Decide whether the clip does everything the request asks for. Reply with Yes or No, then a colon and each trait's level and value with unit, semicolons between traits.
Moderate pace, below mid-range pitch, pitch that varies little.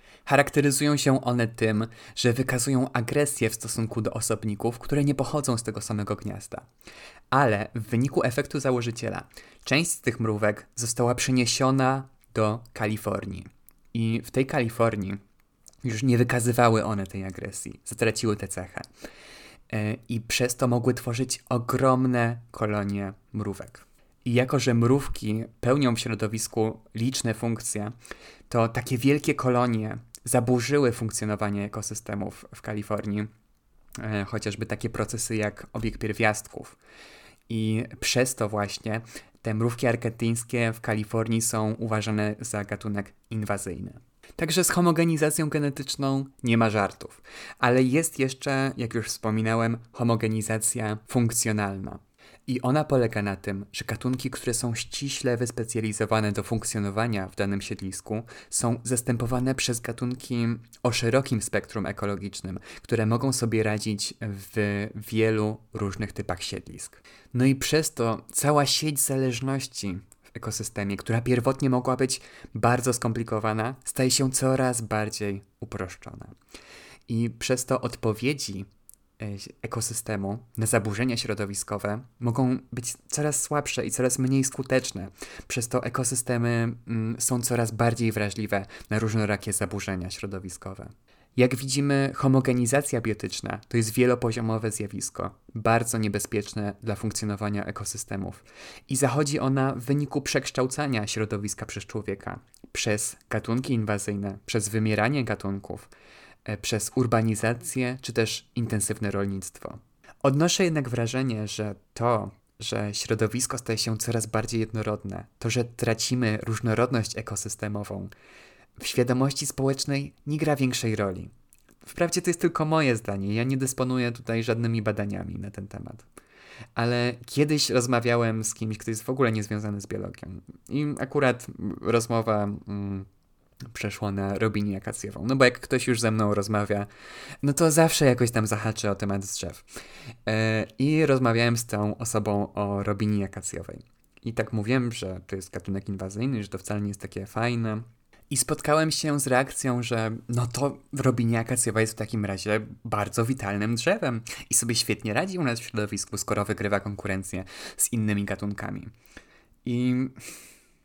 No: average, 130 wpm; low, 115 Hz; average, 3.1 semitones